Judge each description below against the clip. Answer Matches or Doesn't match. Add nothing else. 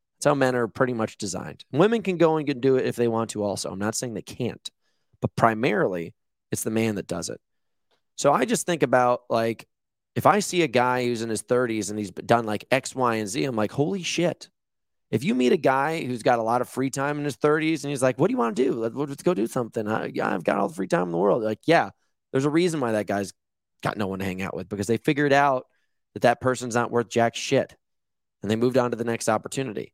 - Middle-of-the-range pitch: Doesn't match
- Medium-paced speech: Doesn't match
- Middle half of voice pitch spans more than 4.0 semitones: Matches